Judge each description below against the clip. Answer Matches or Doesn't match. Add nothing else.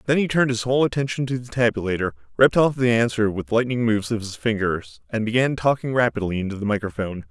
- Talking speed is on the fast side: Matches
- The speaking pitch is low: Matches